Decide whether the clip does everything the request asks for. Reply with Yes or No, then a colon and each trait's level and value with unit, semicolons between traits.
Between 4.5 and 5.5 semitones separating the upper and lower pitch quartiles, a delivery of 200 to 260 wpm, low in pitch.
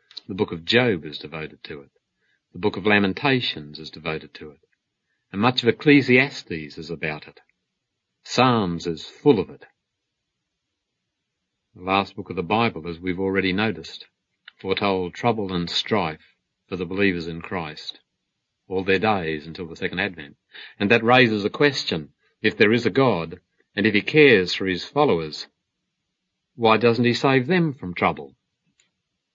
No: average, 5.1 semitones; average, 160 wpm; very low, 95 Hz